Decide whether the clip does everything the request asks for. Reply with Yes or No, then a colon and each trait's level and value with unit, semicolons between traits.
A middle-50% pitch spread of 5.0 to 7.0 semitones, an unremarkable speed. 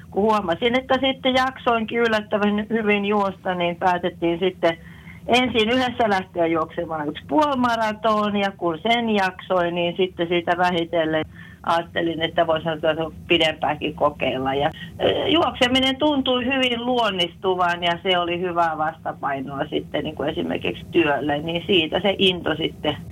Yes: average, 5.3 semitones; average, 130 wpm